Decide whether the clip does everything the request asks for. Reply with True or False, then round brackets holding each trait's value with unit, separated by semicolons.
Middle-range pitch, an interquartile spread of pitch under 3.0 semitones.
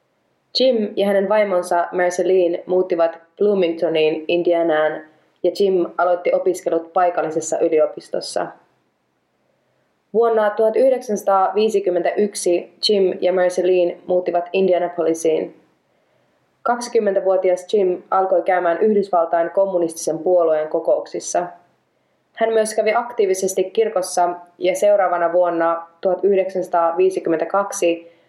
True (180 Hz; 2.6 semitones)